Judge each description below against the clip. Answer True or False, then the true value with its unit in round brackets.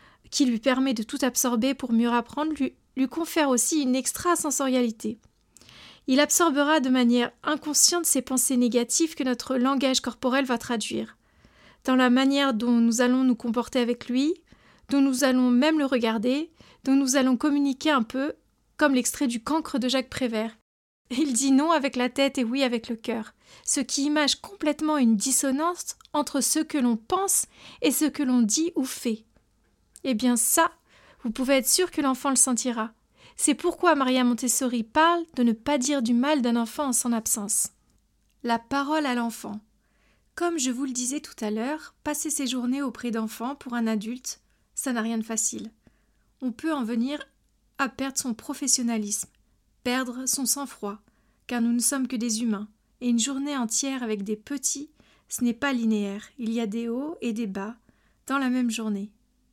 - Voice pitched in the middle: False (260 Hz)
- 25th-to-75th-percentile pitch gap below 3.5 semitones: True (3.1 semitones)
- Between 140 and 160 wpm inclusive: False (180 wpm)